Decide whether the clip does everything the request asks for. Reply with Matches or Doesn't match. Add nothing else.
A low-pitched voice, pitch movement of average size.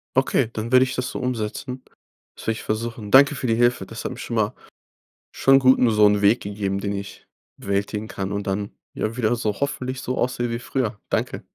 Matches